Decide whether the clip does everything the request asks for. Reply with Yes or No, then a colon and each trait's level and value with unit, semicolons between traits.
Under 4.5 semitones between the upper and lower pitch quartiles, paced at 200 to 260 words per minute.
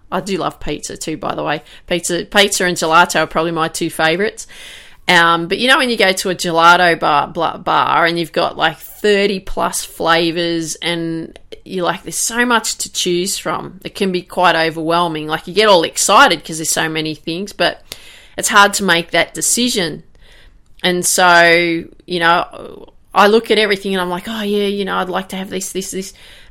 Yes: average, 3.3 semitones; fast, 205 wpm